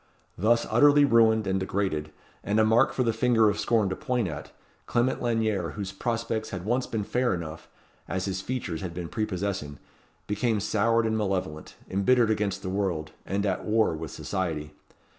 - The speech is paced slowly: No, average, 175 wpm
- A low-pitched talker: Yes, low, 105 Hz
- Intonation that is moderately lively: Yes, average, 3.6 semitones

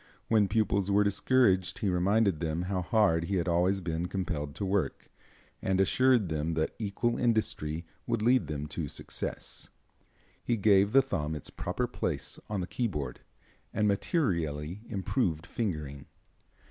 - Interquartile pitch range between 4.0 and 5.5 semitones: Yes, average, 4.6 semitones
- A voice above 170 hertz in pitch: No, very low, 95 Hz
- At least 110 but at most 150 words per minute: Yes, average, 145 wpm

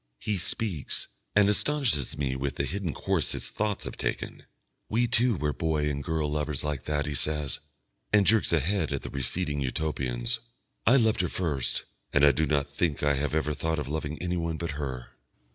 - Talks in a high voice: No, very low, 75 Hz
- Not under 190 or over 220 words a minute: Yes, average, 195 wpm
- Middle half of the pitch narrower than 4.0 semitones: No, average, 4.3 semitones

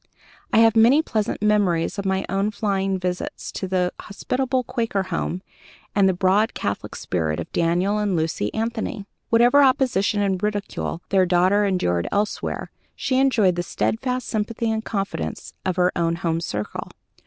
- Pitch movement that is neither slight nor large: Yes, average, 3.7 semitones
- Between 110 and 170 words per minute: Yes, average, 155 wpm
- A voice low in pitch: No, high, 200 Hz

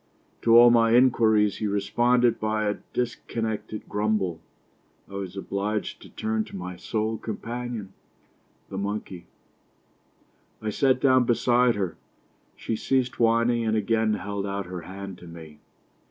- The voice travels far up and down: No, average, 3.0 semitones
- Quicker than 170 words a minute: No, average, 140 wpm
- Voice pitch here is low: Yes, low, 110 Hz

